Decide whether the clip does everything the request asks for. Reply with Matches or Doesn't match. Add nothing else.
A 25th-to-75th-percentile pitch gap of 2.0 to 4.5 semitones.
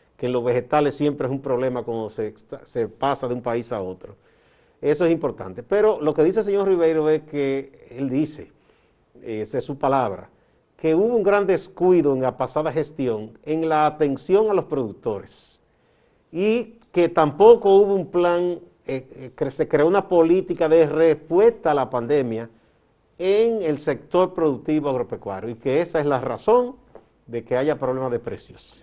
Doesn't match